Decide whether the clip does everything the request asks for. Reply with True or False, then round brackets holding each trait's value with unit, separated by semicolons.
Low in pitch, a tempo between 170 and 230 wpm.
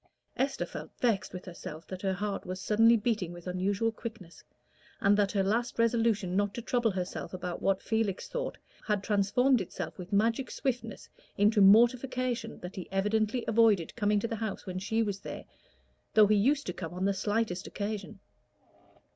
False (205 Hz; 175 wpm)